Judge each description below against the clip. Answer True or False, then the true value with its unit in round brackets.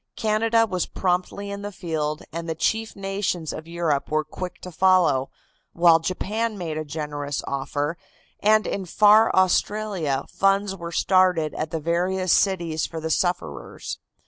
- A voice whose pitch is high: False (175 Hz)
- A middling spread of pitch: True (3.9 semitones)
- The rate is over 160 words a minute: False (150 wpm)